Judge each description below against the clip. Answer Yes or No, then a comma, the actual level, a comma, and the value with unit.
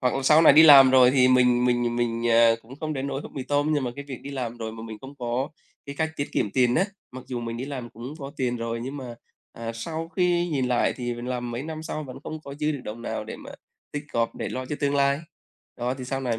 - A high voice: No, low, 130 Hz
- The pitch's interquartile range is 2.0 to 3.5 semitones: Yes, average, 2.9 semitones